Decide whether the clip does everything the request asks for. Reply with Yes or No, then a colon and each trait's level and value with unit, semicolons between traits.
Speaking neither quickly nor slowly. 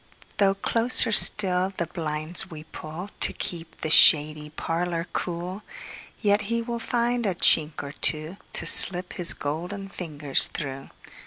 No: slow, 130 wpm